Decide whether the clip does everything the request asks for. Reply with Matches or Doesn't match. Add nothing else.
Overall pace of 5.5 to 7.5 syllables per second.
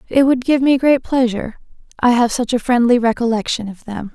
Matches